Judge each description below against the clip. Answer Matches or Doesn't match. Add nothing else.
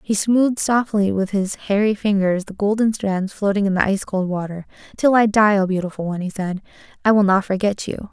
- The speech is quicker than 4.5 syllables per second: Matches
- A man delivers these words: Doesn't match